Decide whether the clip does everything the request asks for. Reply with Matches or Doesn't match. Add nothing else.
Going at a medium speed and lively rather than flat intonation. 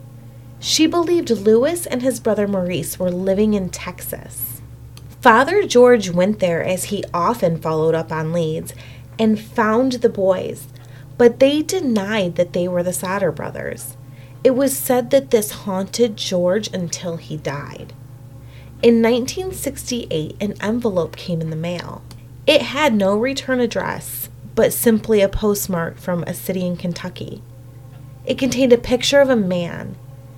Matches